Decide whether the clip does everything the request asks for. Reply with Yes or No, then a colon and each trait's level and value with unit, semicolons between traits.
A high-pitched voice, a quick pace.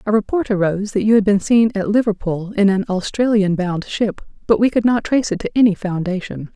Yes: high, 205 Hz; fast, 220 wpm